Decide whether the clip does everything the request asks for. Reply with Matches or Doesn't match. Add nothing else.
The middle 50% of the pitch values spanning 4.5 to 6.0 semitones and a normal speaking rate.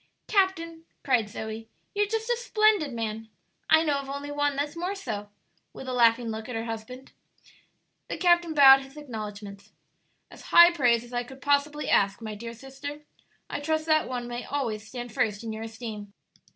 Matches